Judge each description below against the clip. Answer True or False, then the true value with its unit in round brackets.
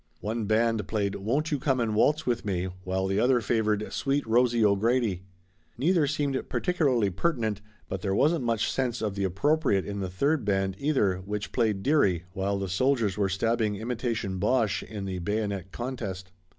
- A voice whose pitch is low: True (110 Hz)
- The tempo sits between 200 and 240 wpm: False (175 wpm)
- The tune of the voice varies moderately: True (4.7 semitones)